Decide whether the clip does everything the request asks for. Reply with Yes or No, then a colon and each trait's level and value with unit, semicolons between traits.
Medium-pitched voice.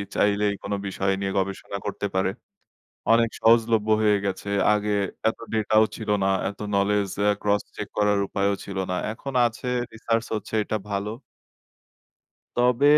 No: low, 105 Hz